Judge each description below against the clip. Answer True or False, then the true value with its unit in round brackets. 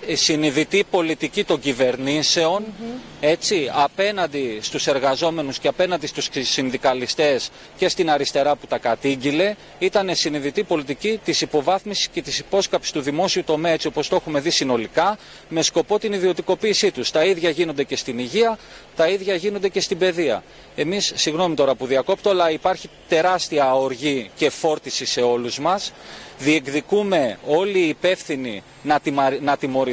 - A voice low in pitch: False (160 Hz)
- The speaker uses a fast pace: False (150 wpm)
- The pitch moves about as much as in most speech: True (4.8 semitones)